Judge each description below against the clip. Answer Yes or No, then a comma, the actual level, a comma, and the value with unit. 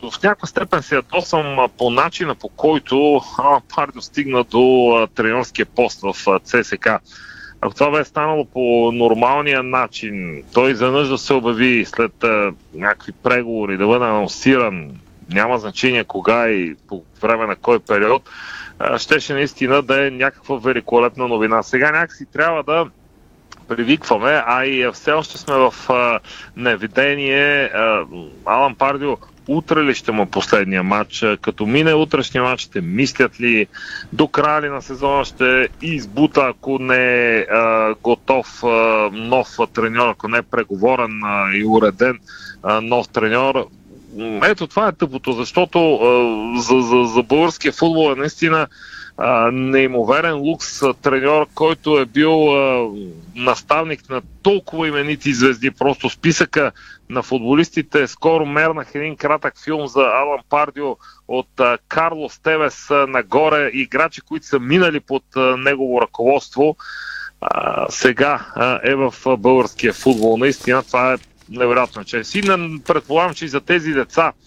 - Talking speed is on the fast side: No, average, 145 wpm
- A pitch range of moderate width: Yes, average, 3.7 semitones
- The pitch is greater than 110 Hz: Yes, low, 135 Hz